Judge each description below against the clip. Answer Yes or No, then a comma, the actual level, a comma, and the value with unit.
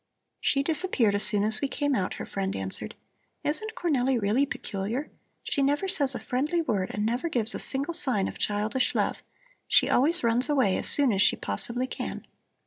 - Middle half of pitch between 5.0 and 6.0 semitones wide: Yes, wide, 5.6 semitones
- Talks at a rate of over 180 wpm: Yes, average, 190 wpm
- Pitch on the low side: No, very high, 255 Hz